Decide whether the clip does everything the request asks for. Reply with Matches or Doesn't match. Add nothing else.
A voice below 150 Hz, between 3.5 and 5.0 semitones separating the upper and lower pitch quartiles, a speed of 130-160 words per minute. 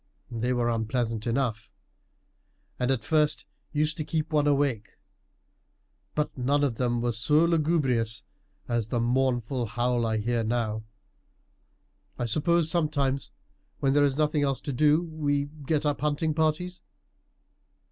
Matches